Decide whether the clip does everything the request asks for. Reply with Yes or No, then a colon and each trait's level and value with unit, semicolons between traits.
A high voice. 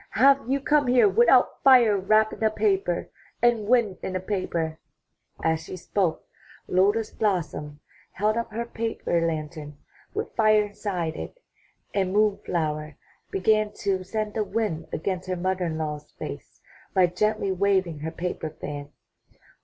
Yes: high, 195 Hz